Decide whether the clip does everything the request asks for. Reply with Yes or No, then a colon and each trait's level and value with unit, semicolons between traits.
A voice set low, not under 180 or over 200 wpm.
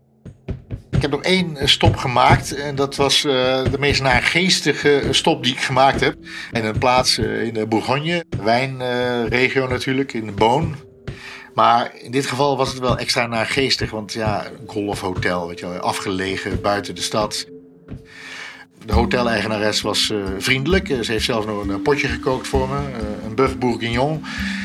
No: low, 125 Hz; average, 150 wpm